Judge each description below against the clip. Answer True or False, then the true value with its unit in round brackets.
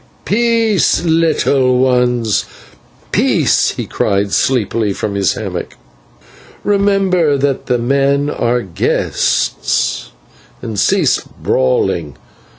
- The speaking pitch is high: False (130 Hz)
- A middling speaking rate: False (90 wpm)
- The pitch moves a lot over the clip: True (7.8 semitones)